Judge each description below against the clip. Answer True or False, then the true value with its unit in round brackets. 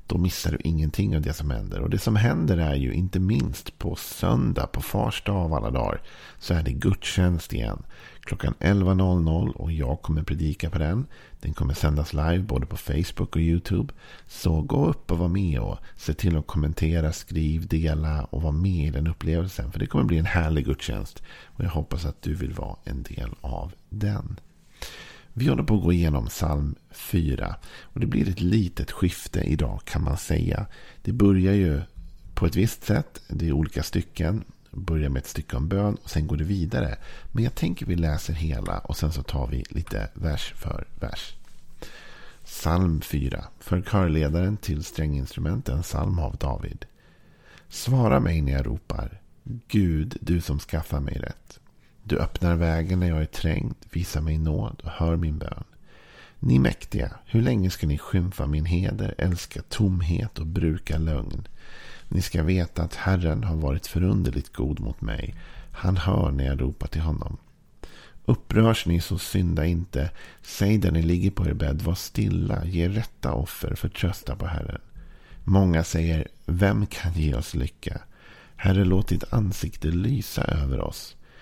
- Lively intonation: False (3.5 semitones)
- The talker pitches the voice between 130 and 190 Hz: False (85 Hz)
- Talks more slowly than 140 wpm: False (175 wpm)